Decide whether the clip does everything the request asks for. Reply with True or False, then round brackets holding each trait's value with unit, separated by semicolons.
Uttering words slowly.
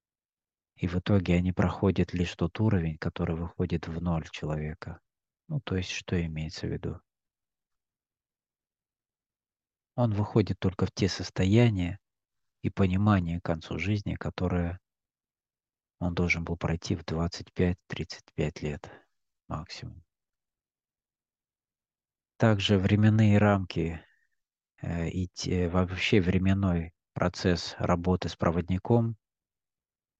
True (100 wpm)